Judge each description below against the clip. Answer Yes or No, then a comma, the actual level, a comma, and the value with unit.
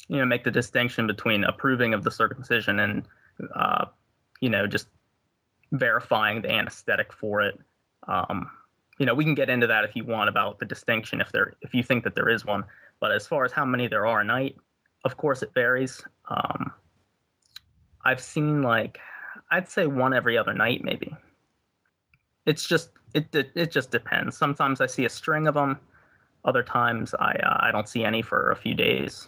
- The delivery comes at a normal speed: Yes, average, 195 wpm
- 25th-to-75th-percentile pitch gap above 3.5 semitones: Yes, average, 3.9 semitones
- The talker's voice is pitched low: Yes, low, 130 Hz